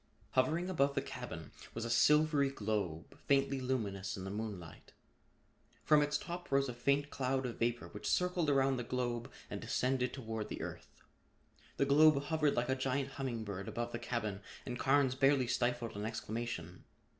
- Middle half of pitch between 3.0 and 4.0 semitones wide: Yes, average, 3.6 semitones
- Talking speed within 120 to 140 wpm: No, average, 170 wpm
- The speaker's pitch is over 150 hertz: No, low, 130 Hz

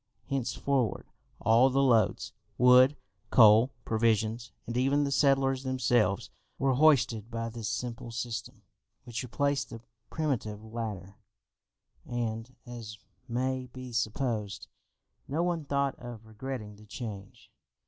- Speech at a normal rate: No, slow, 120 wpm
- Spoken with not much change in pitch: No, average, 3.0 semitones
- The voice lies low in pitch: Yes, low, 120 Hz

